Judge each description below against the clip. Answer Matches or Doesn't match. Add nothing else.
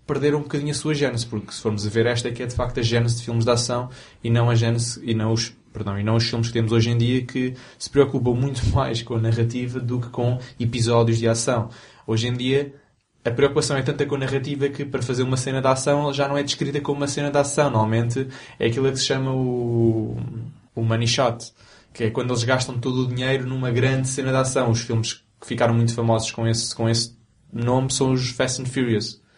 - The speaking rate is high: Matches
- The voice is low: Matches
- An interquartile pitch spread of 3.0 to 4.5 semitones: Doesn't match